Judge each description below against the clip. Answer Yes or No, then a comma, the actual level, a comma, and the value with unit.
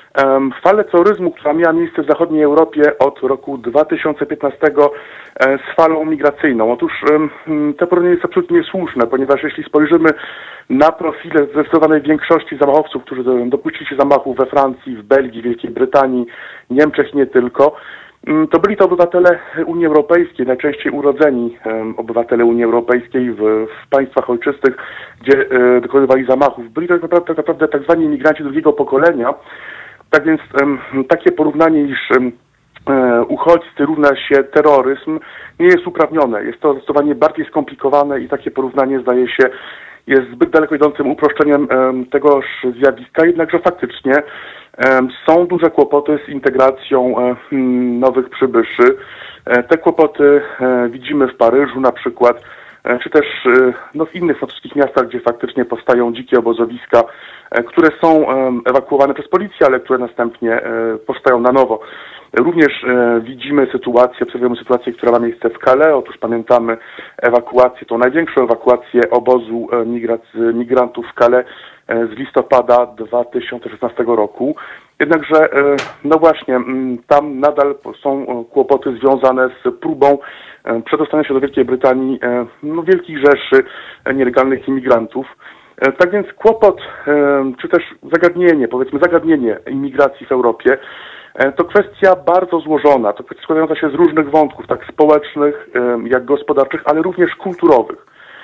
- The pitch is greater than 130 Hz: Yes, medium, 140 Hz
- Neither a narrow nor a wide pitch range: Yes, average, 3.7 semitones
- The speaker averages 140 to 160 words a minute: No, average, 130 wpm